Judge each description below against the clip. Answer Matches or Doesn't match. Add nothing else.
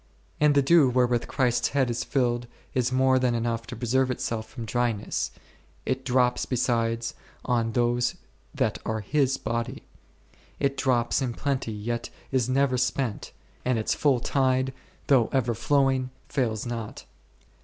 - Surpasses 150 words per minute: Doesn't match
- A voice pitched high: Doesn't match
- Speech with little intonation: Matches